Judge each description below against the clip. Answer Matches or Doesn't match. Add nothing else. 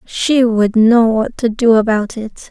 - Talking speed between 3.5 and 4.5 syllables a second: Matches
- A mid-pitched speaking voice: Doesn't match